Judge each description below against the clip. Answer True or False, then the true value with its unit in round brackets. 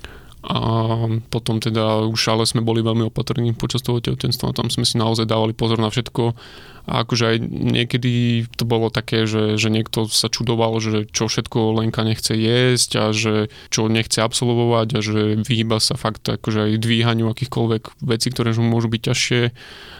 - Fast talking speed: True (175 wpm)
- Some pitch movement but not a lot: False (1.2 semitones)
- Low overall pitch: True (115 Hz)